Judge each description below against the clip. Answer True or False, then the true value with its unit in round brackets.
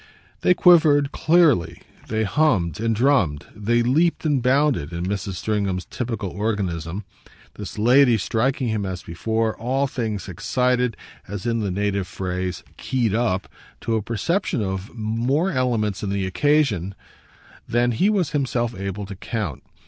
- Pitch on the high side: False (110 Hz)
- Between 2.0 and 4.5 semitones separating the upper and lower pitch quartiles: False (4.9 semitones)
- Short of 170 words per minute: True (145 wpm)